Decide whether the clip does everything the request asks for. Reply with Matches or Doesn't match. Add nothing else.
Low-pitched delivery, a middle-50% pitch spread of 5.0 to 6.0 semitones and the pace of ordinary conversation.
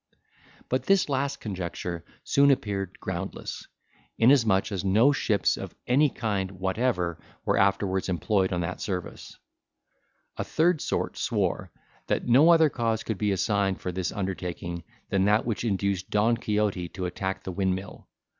Doesn't match